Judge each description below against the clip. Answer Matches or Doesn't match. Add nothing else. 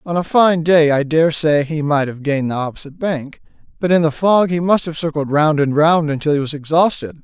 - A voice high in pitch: Doesn't match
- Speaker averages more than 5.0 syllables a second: Matches